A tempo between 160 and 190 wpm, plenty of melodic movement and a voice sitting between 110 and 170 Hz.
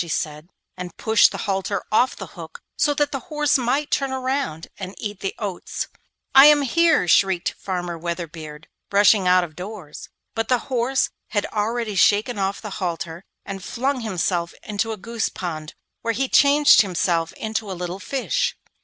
No: average, 170 wpm; wide, 6.2 semitones; high, 205 Hz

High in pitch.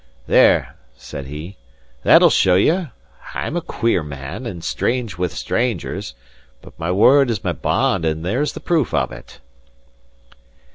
No: very low, 95 Hz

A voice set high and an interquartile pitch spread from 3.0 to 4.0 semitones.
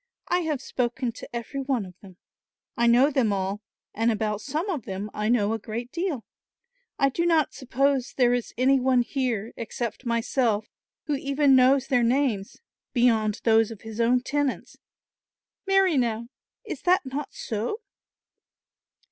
Yes: high, 245 Hz; average, 3.7 semitones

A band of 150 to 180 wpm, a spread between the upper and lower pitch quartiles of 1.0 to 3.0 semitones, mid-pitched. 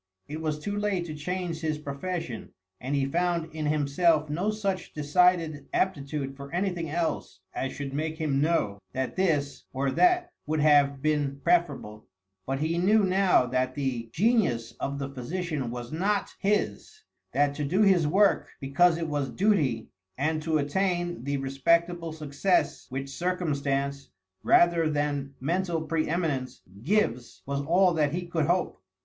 No: average, 155 wpm; average, 4.1 semitones; medium, 155 Hz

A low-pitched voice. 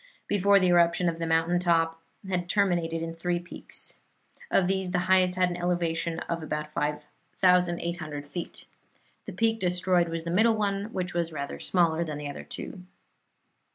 No: medium, 175 Hz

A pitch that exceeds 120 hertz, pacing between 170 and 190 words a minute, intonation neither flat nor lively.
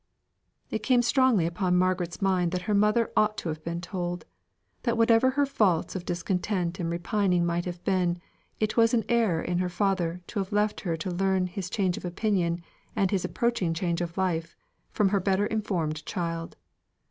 Yes: medium, 185 Hz; average, 185 wpm; average, 3.3 semitones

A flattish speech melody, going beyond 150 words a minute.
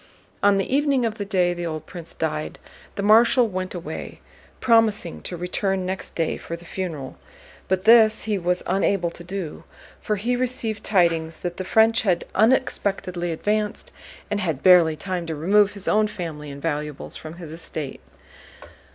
No: average, 4.0 semitones; average, 170 wpm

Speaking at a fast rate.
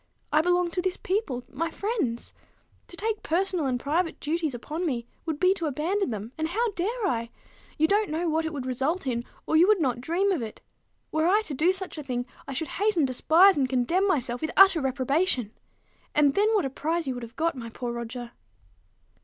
Yes: fast, 215 wpm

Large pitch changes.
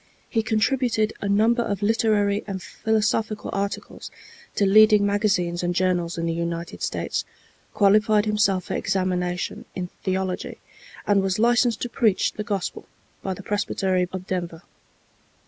No: average, 2.8 semitones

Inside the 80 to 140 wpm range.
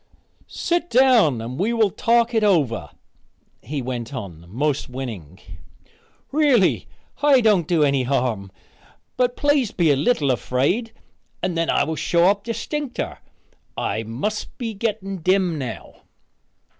Yes: slow, 135 wpm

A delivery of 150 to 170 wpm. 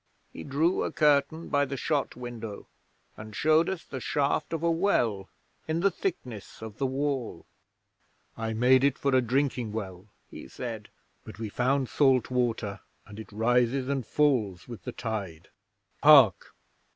Yes: average, 160 wpm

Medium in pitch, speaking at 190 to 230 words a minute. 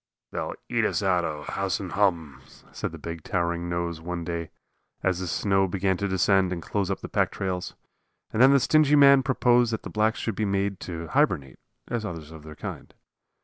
No: very low, 95 Hz; fast, 205 wpm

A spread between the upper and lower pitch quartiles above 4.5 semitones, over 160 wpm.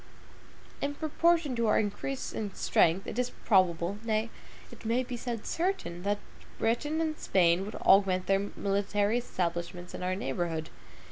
No: average, 5.0 semitones; average, 150 wpm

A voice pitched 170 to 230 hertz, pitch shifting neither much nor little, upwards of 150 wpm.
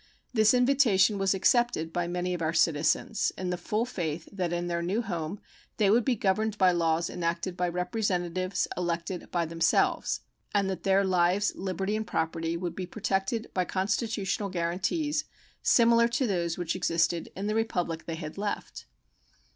Yes: medium, 185 Hz; average, 3.6 semitones; average, 165 wpm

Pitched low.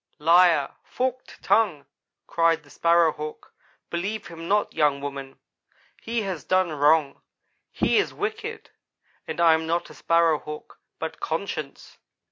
No: medium, 165 Hz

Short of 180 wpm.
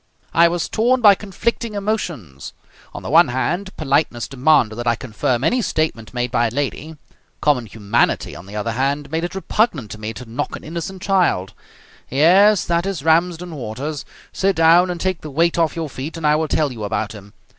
No: average, 200 wpm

